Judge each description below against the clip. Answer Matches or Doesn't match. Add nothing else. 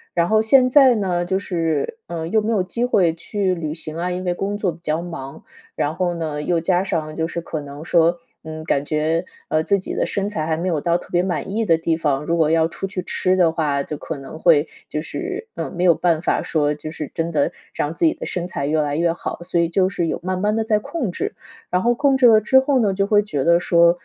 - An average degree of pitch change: Matches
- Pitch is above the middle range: Doesn't match